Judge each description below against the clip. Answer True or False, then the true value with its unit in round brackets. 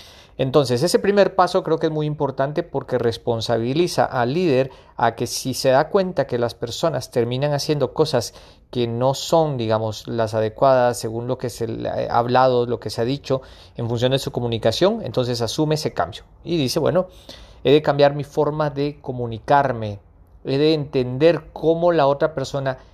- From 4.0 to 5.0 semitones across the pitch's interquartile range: True (4.4 semitones)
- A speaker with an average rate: True (180 wpm)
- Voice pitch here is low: True (130 Hz)